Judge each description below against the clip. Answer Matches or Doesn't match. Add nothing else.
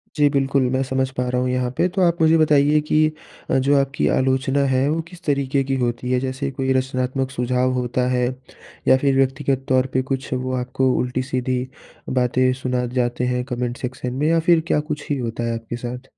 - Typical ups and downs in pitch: Doesn't match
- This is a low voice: Matches